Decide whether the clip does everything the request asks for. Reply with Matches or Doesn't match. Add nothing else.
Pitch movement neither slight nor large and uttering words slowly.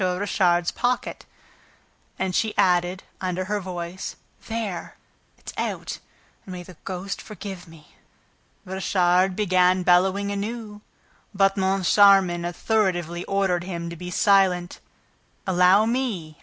Doesn't match